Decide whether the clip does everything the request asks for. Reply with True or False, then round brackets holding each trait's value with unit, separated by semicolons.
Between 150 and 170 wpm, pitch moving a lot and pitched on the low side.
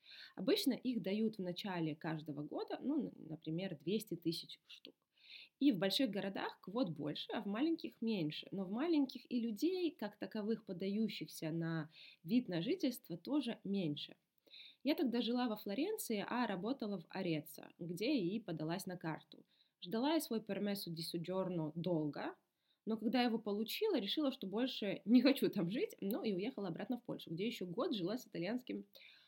False (160 wpm; 6.6 semitones; 210 Hz)